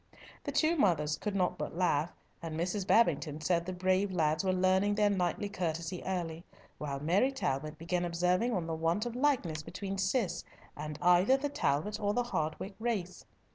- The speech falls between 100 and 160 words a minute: No, average, 175 wpm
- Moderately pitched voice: Yes, medium, 180 Hz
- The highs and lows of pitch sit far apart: No, average, 3.9 semitones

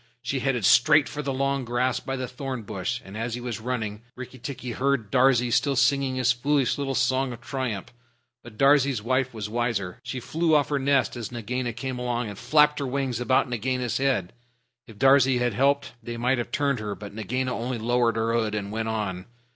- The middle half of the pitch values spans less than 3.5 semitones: Yes, average, 2.8 semitones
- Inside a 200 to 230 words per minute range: Yes, fast, 205 wpm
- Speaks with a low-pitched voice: Yes, low, 125 Hz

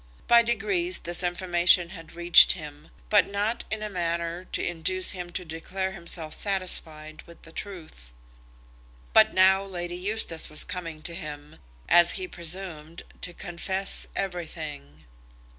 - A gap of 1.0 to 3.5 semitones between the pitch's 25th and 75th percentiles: Yes, average, 2.7 semitones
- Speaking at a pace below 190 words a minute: Yes, average, 140 wpm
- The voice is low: No, medium, 175 Hz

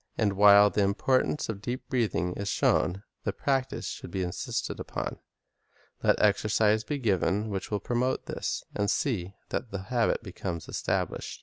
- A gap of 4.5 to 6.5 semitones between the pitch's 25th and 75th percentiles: No, average, 3.4 semitones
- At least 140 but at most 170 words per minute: Yes, average, 160 wpm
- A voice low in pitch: Yes, low, 105 Hz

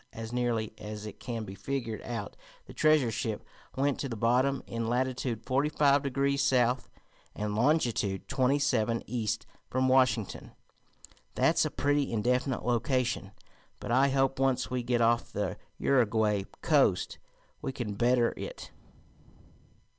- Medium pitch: No, low, 125 Hz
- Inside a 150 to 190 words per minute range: No, average, 140 wpm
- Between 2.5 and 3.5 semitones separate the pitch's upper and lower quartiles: Yes, average, 3.1 semitones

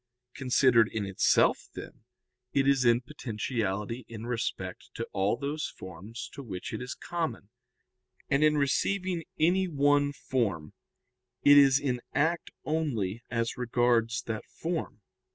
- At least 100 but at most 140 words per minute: Yes, slow, 135 wpm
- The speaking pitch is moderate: No, low, 125 Hz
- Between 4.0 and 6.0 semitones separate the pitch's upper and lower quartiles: Yes, average, 4.3 semitones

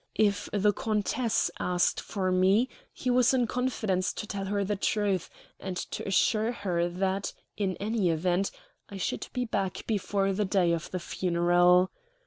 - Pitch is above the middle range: Yes, high, 195 Hz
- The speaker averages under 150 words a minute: No, average, 160 wpm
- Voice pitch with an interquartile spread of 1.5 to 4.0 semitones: Yes, narrow, 2.6 semitones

